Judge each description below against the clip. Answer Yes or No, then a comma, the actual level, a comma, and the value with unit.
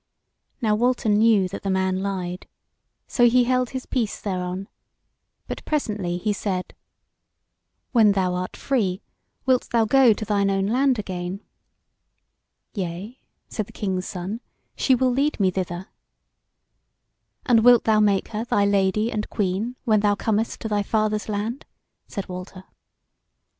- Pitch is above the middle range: Yes, high, 210 Hz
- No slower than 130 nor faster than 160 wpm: Yes, average, 145 wpm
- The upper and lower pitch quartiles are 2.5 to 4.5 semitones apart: Yes, average, 3.4 semitones